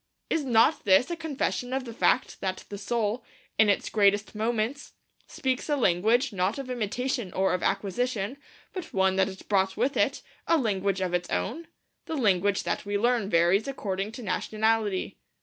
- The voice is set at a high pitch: Yes, high, 215 Hz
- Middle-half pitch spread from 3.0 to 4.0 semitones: No, average, 4.6 semitones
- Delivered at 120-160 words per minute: No, average, 175 wpm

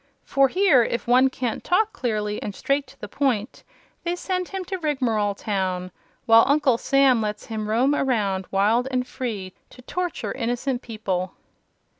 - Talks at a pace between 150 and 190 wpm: Yes, average, 160 wpm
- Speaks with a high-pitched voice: Yes, high, 245 Hz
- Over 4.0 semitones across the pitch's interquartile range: Yes, average, 4.6 semitones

